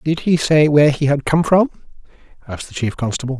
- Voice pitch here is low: No, medium, 145 Hz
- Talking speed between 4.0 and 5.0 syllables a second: No, 6.4 syllables/s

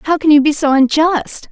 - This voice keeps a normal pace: No, fast, 235 wpm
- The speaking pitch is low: No, very high, 300 Hz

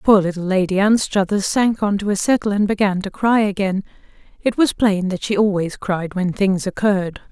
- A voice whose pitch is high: Yes, high, 200 Hz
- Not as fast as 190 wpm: No, average, 195 wpm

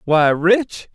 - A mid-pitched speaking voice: Yes, medium, 175 Hz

